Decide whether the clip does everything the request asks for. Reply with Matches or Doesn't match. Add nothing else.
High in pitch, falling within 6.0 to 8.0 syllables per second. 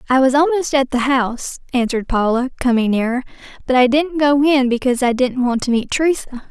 Matches